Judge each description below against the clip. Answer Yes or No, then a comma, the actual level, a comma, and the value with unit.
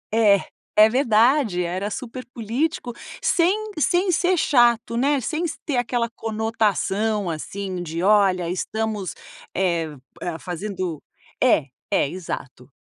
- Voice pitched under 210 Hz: No, high, 220 Hz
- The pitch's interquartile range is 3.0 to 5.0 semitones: No, wide, 5.4 semitones